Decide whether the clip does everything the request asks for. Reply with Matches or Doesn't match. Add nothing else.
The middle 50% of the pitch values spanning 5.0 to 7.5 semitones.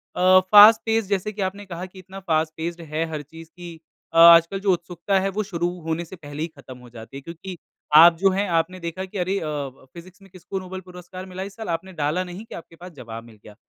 Doesn't match